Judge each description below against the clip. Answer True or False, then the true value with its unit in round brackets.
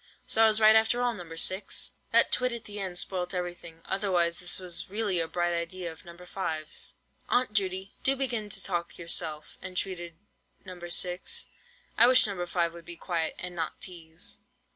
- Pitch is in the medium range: True (180 Hz)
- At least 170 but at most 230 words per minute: True (185 wpm)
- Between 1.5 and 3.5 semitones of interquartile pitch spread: True (3.2 semitones)